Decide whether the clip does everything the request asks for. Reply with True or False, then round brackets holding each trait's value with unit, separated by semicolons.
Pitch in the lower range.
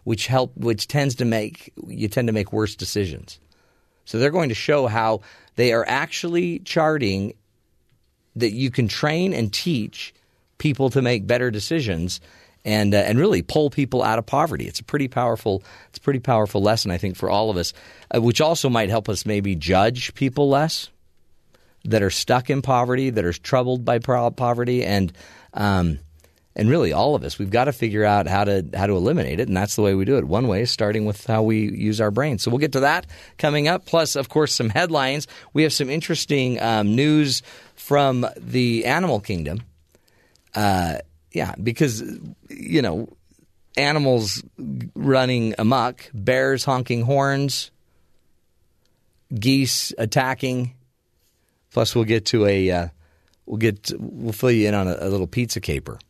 True (115 Hz)